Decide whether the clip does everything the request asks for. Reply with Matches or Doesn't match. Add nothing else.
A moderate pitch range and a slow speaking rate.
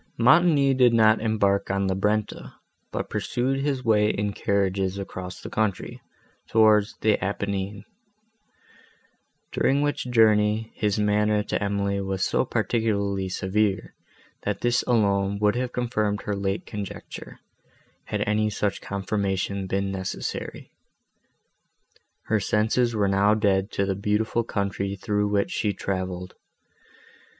Doesn't match